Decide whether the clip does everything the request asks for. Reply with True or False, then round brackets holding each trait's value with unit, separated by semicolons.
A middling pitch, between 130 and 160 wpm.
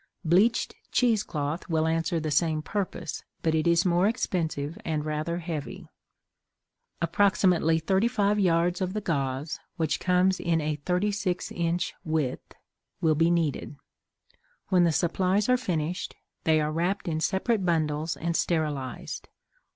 True (170 Hz; 145 wpm)